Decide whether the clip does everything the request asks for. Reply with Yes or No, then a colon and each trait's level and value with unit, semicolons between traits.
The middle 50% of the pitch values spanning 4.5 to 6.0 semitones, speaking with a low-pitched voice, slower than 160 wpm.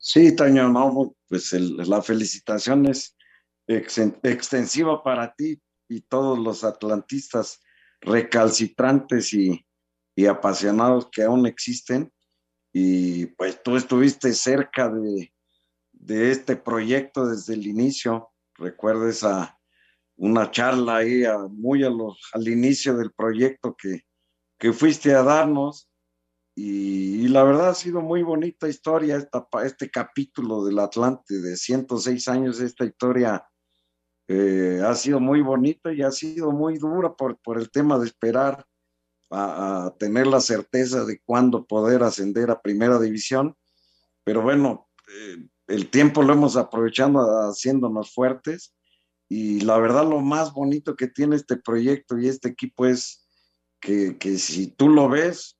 Yes: average, 5.2 semitones; low, 115 Hz; average, 140 wpm